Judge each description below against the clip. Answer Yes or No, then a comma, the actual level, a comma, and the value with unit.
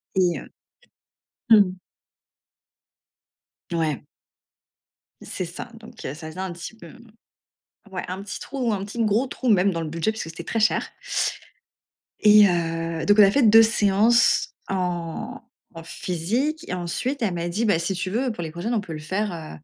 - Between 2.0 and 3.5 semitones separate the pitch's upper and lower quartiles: No, average, 4.7 semitones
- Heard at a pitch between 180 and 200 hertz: Yes, high, 190 Hz